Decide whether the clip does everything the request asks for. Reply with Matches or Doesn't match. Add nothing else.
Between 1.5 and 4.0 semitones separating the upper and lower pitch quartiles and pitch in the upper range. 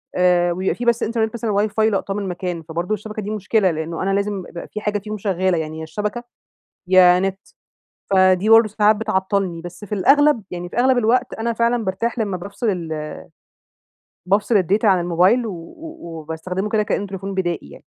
Matches